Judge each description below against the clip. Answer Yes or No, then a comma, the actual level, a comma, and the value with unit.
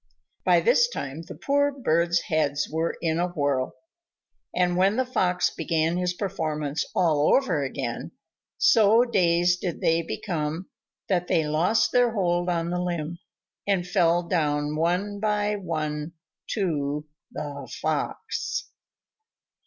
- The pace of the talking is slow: Yes, slow, 130 wpm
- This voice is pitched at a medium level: Yes, medium, 175 Hz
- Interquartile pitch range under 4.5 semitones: Yes, average, 3.8 semitones